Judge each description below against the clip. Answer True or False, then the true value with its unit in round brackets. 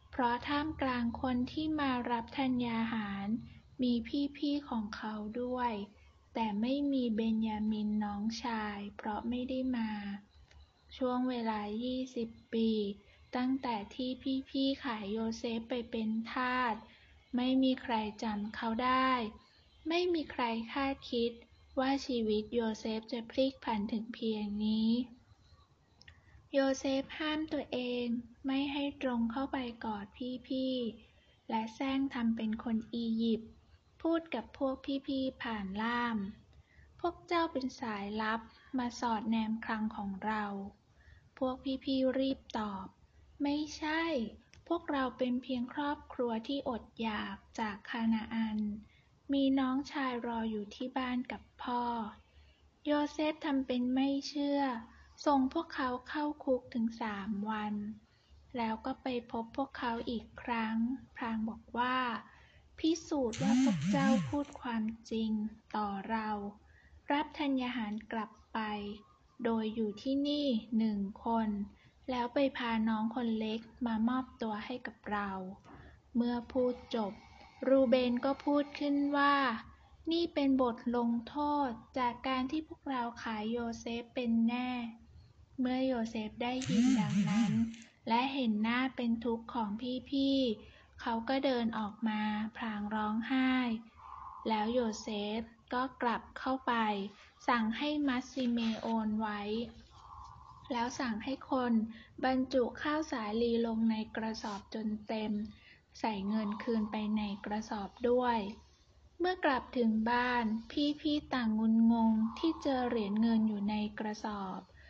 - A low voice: False (240 Hz)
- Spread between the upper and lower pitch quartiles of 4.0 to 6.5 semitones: False (3.2 semitones)